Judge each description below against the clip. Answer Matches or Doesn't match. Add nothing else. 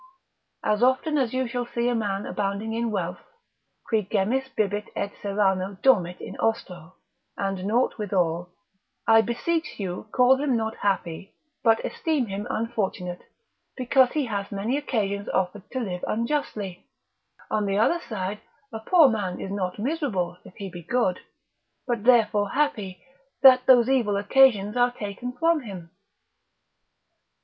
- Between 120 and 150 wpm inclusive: Matches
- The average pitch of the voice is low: Doesn't match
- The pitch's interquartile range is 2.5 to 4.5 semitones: Matches